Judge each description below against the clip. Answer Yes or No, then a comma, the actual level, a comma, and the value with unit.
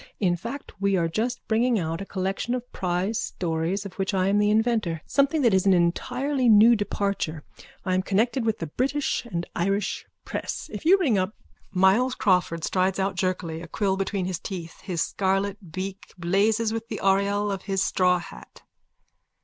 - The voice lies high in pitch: Yes, high, 195 Hz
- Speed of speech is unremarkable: Yes, average, 180 wpm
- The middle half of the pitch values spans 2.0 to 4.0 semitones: Yes, average, 3.3 semitones